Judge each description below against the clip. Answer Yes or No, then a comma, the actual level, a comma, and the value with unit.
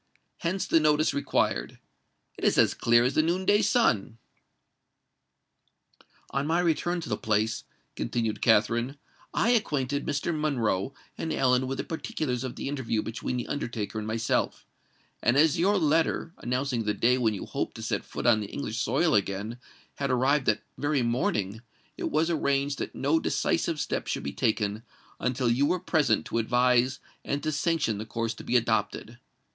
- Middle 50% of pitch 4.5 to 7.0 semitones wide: Yes, average, 5.1 semitones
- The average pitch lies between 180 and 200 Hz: No, low, 130 Hz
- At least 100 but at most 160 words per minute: No, average, 175 wpm